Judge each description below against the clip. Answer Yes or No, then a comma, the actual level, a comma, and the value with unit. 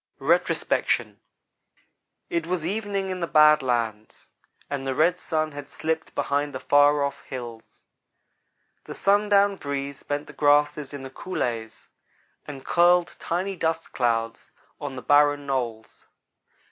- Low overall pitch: No, medium, 145 Hz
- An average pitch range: Yes, average, 4.1 semitones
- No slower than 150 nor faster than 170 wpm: No, slow, 135 wpm